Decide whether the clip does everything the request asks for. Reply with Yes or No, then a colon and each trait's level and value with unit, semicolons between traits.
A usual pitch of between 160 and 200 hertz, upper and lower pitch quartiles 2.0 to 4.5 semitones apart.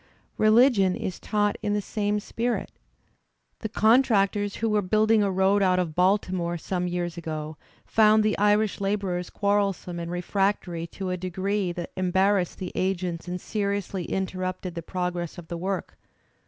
Yes: high, 190 Hz; narrow, 2.6 semitones